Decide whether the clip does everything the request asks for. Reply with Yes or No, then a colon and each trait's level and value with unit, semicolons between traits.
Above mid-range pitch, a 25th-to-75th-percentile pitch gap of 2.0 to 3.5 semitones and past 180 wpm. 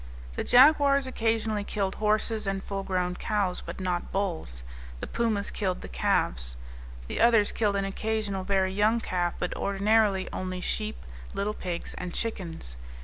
No: high, 200 Hz; average, 3.1 semitones; average, 150 wpm